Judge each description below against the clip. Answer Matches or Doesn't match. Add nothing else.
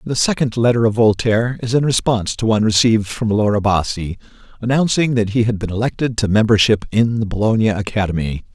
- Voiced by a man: Matches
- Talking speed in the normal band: Matches